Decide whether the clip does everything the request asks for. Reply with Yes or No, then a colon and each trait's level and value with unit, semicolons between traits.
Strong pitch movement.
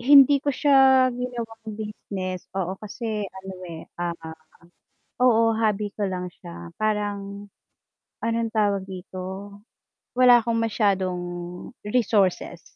No: average, 3.4 semitones